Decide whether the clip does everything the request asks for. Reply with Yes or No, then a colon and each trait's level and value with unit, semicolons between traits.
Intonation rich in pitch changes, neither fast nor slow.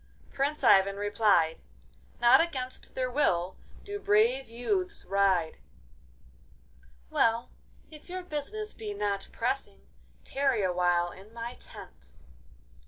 No: wide, 6.2 semitones; slow, 105 wpm